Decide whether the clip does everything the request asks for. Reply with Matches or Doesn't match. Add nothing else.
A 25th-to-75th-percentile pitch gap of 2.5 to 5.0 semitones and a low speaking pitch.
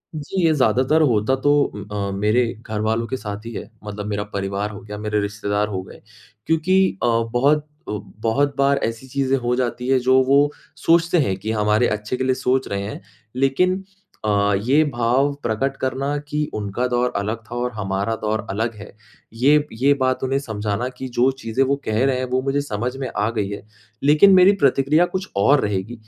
Matches